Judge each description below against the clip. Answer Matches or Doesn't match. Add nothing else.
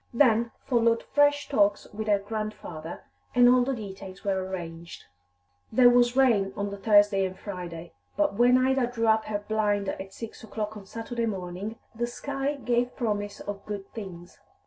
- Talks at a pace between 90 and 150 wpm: Doesn't match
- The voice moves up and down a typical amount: Matches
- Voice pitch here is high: Matches